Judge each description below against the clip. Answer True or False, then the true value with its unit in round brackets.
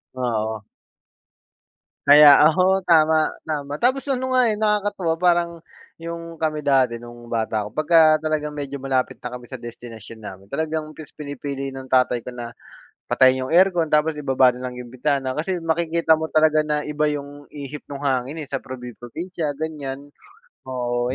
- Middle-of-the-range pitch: True (145 Hz)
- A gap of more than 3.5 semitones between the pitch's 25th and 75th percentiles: True (3.9 semitones)